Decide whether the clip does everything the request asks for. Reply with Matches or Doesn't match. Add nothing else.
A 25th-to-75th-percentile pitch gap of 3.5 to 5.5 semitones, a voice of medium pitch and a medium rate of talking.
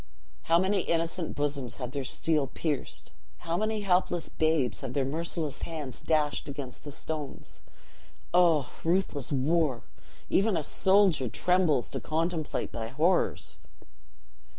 Doesn't match